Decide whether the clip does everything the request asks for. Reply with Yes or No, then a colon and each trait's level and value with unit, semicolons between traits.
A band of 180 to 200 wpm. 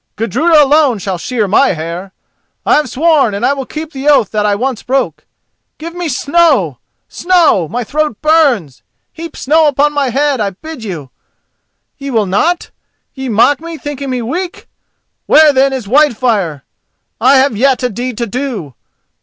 No: average, 165 wpm